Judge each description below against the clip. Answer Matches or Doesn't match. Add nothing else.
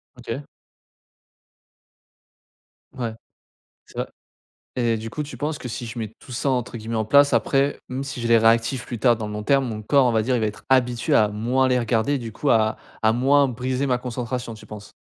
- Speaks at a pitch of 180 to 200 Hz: Doesn't match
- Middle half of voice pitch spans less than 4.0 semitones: Matches